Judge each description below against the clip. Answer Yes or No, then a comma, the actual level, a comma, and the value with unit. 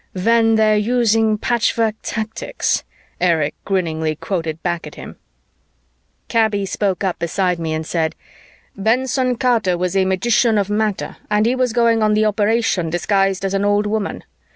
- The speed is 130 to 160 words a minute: Yes, average, 155 wpm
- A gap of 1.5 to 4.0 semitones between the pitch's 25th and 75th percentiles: Yes, average, 3.7 semitones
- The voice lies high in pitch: Yes, high, 205 Hz